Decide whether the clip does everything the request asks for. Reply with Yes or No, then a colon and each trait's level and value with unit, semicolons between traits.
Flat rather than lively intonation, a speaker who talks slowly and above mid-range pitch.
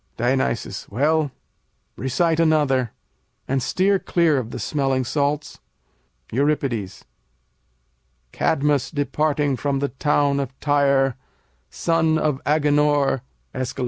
No: narrow, 2.2 semitones; slow, 100 wpm; medium, 145 Hz